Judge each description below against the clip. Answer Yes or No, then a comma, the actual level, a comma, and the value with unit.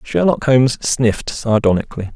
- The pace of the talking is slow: Yes, slow, 110 wpm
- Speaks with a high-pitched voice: No, low, 120 Hz